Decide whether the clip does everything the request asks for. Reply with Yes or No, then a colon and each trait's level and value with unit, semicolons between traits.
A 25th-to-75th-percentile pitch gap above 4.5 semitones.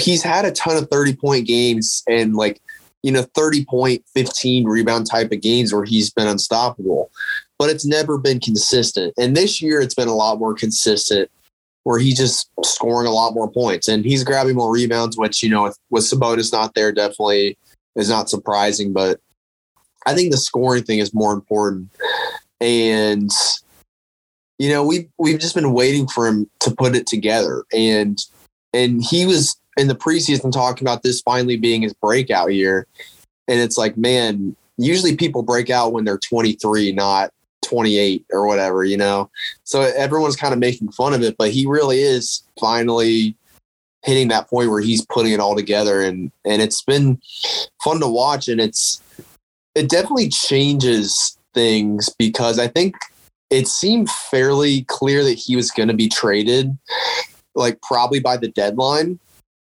No: average, 4.0 semitones